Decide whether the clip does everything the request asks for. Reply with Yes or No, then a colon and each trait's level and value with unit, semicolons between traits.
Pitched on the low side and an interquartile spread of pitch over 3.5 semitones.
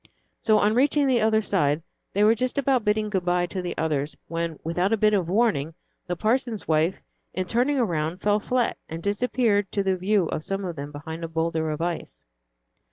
No: high, 195 Hz; average, 4.9 semitones